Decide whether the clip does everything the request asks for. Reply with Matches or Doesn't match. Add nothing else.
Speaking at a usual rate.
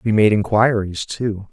Matches